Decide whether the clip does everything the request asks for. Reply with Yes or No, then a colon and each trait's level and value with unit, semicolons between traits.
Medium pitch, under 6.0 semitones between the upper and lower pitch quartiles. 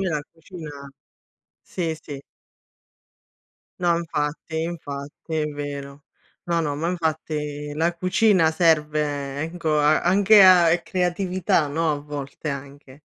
Yes: medium, 155 Hz; average, 2.8 semitones